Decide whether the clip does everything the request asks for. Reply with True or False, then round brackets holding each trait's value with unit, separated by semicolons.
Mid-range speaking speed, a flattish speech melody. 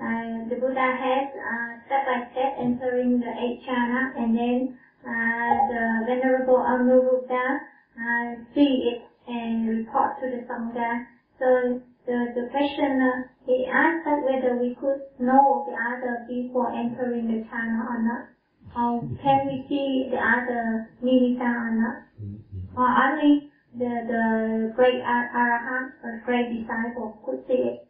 False (150 wpm; 1.7 semitones)